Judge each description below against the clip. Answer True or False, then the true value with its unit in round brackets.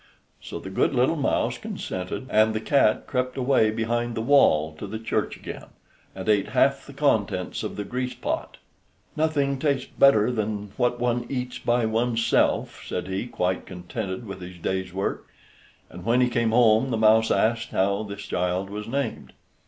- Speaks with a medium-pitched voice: False (110 Hz)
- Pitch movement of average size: True (4.1 semitones)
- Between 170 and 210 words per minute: True (175 wpm)